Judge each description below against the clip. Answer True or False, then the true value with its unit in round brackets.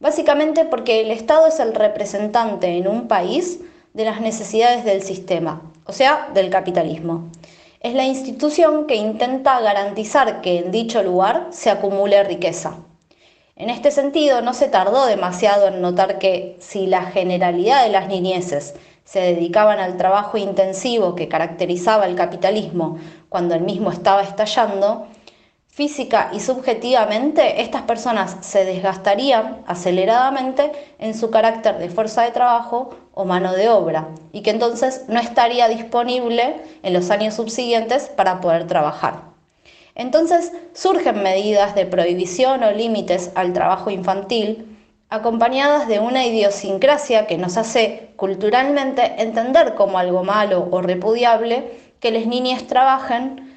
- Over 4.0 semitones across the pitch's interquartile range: True (4.6 semitones)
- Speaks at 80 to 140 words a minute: True (135 wpm)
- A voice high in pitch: True (215 Hz)